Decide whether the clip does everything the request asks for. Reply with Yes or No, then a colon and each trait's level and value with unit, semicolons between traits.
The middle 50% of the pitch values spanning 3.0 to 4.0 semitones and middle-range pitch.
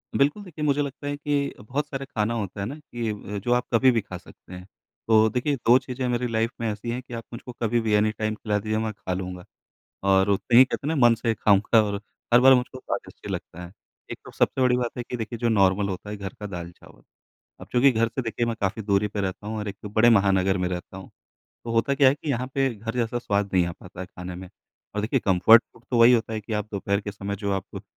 No: average, 3.7 semitones; low, 110 Hz